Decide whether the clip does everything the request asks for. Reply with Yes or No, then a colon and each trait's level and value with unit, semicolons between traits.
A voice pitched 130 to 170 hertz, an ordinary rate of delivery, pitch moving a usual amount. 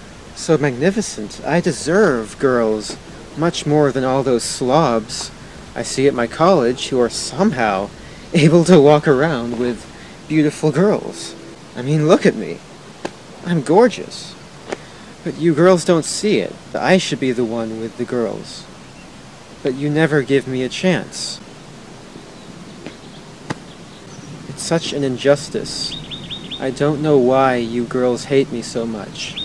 Yes: medium, 140 Hz; average, 140 wpm; average, 4.7 semitones